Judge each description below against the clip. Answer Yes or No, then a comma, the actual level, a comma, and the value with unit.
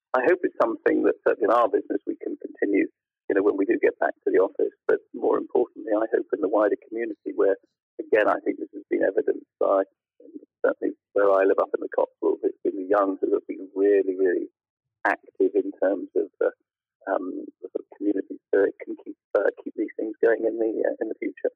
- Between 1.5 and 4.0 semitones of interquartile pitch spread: No, average, 4.6 semitones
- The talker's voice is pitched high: Yes, very high, 390 Hz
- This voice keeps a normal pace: No, fast, 230 wpm